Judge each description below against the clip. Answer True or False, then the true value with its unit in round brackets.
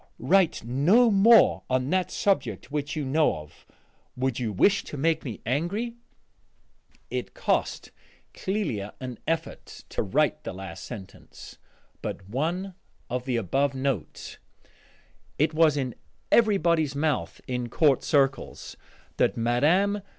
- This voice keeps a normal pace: False (130 wpm)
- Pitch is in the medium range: True (145 Hz)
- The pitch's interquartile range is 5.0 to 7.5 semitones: True (5.6 semitones)